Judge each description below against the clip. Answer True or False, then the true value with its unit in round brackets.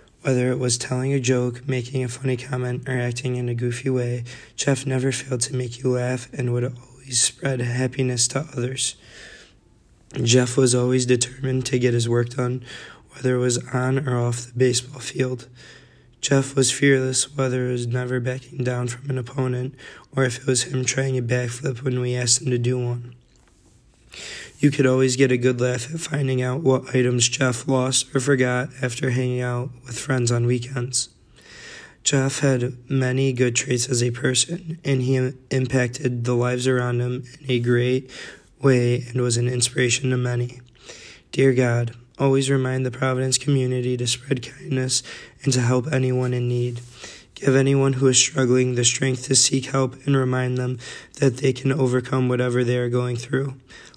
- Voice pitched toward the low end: True (125 Hz)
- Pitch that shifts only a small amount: True (1.2 semitones)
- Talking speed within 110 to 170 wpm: False (180 wpm)